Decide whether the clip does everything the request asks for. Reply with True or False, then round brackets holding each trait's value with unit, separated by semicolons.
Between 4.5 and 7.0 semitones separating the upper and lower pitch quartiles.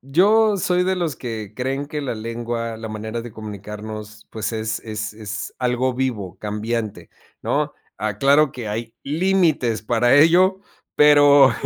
True (5.0 semitones)